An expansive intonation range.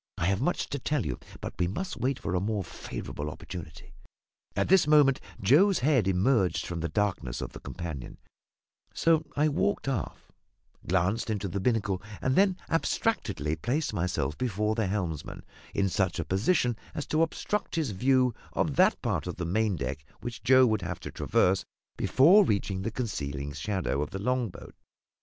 Yes: wide, 7.0 semitones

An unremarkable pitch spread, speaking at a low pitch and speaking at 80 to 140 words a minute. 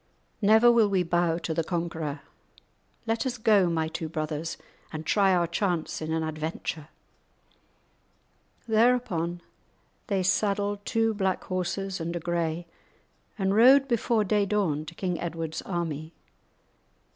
No: average, 4.1 semitones; medium, 175 Hz; slow, 135 wpm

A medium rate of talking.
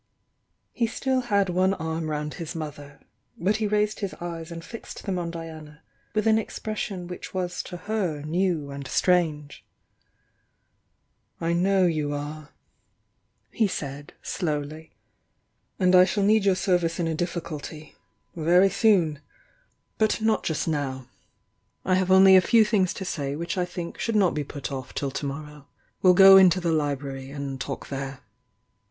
Yes: average, 170 wpm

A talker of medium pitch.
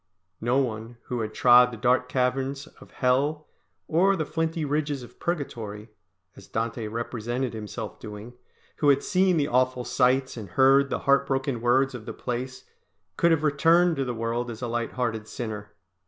No: low, 125 Hz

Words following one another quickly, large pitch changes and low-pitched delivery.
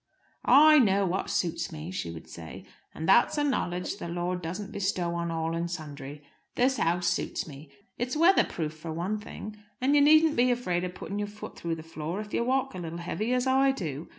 No: fast, 215 wpm; wide, 6.5 semitones; medium, 180 Hz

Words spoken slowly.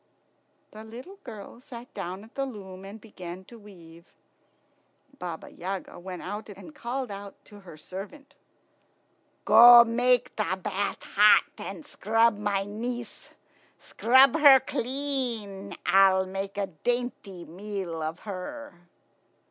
Yes: slow, 125 wpm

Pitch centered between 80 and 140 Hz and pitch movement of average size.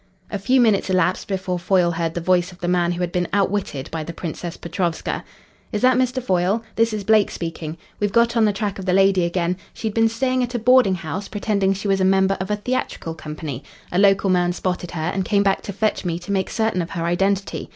No: high, 190 Hz; average, 3.1 semitones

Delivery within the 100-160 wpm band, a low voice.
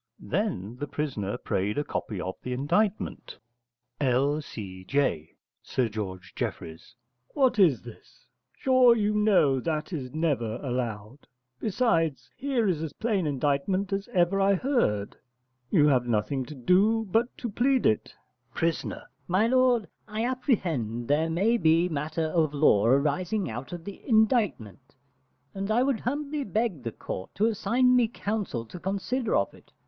No: average, 150 wpm; medium, 165 Hz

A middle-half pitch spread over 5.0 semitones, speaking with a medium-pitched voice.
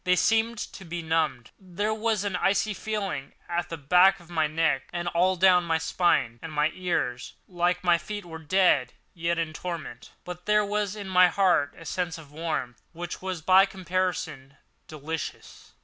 No: average, 2.9 semitones; medium, 175 Hz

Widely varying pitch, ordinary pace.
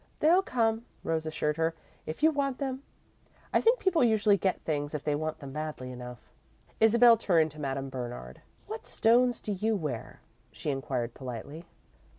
Yes: wide, 8.8 semitones; average, 165 wpm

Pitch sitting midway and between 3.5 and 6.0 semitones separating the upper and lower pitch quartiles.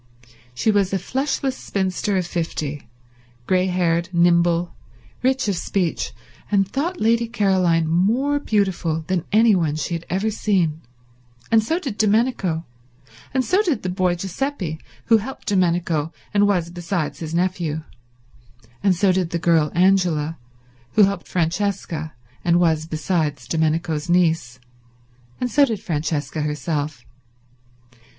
Yes: medium, 180 Hz; average, 4.0 semitones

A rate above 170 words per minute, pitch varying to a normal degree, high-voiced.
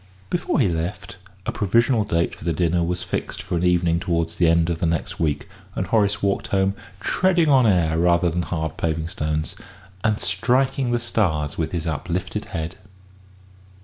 No: average, 180 wpm; average, 3.9 semitones; very low, 90 Hz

